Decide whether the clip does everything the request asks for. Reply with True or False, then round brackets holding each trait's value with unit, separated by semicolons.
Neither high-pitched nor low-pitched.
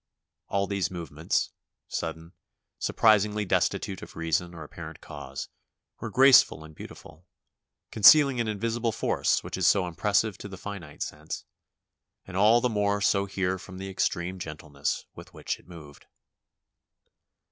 False (95 Hz)